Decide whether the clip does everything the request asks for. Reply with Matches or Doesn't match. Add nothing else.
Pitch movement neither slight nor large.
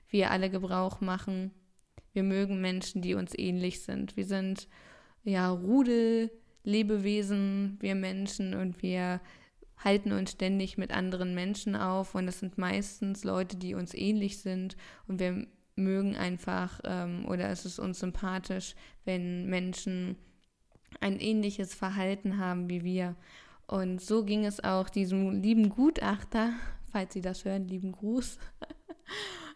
Doesn't match